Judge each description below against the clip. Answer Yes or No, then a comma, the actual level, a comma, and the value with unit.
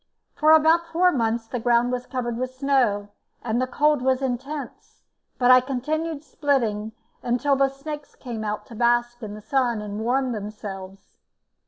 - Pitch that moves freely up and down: No, average, 3.6 semitones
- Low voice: No, very high, 250 Hz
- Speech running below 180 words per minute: Yes, average, 165 wpm